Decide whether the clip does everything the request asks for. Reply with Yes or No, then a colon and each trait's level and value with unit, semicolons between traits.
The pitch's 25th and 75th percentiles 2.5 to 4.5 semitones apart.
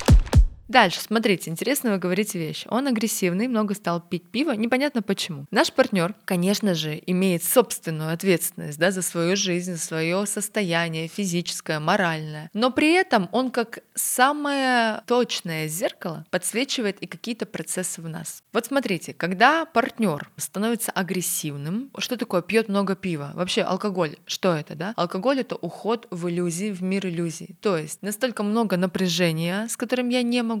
No: average, 5.0 semitones